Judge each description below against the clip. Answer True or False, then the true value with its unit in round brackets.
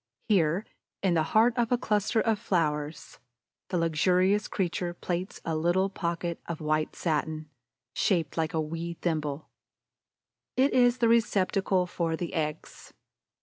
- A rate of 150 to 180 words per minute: False (140 wpm)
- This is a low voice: False (175 Hz)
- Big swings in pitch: False (3.8 semitones)